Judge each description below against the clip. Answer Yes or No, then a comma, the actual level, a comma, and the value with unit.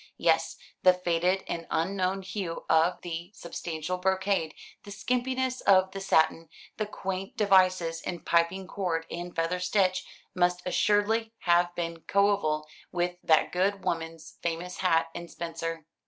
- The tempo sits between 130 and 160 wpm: Yes, average, 140 wpm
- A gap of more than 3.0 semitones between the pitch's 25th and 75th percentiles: No, narrow, 2.6 semitones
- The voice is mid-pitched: Yes, medium, 180 Hz